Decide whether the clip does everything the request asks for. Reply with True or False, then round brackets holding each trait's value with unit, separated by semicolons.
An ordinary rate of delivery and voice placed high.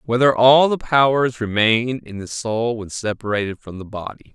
False (180 wpm; 115 Hz)